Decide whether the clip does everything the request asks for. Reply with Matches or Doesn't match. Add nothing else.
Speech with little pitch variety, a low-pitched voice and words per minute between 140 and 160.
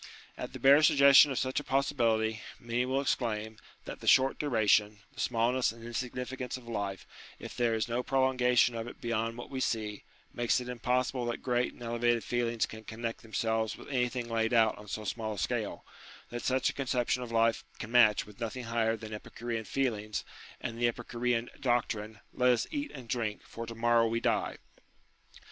Doesn't match